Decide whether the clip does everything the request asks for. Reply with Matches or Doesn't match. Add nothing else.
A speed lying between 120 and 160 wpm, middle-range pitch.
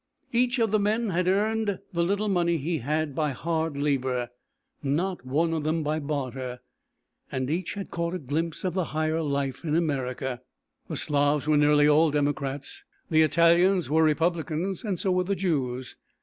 Doesn't match